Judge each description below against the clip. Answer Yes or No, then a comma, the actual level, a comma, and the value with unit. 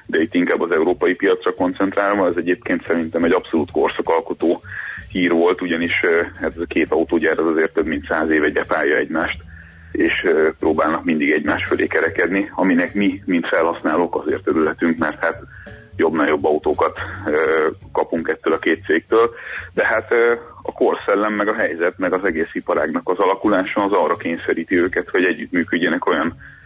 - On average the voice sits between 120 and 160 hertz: No, low, 100 Hz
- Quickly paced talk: Yes, fast, 160 wpm